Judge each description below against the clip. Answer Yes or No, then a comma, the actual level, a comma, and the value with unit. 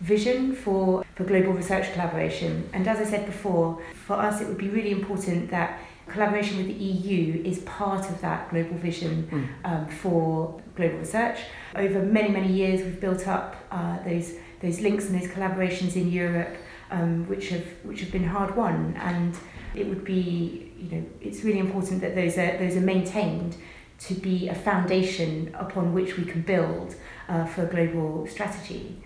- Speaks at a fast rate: No, average, 180 wpm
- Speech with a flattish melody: Yes, narrow, 2.3 semitones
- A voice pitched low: No, medium, 185 Hz